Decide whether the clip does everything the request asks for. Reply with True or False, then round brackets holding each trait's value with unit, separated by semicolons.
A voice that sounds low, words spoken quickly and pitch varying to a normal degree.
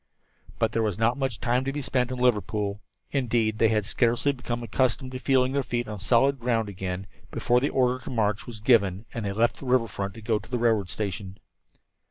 True (115 Hz; 220 wpm; 3.2 semitones)